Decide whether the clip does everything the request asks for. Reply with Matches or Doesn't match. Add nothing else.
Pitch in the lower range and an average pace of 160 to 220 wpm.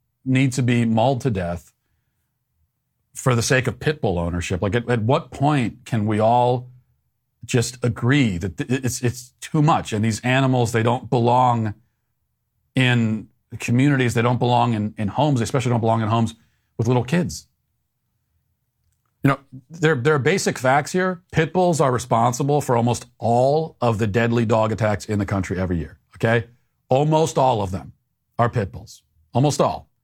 Matches